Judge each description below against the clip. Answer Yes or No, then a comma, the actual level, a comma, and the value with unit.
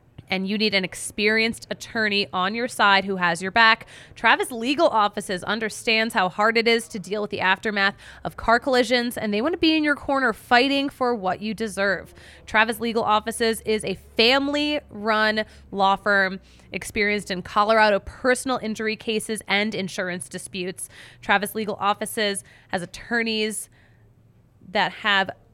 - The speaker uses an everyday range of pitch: Yes, average, 3.0 semitones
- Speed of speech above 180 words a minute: No, average, 155 wpm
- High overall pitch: Yes, high, 215 Hz